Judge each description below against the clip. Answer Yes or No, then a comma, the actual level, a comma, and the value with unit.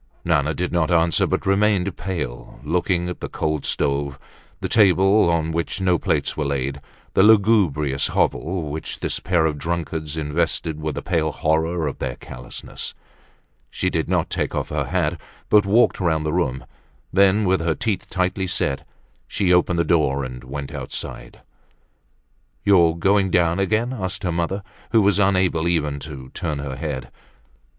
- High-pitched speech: No, very low, 85 Hz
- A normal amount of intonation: Yes, average, 3.9 semitones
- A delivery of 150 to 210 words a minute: Yes, average, 165 wpm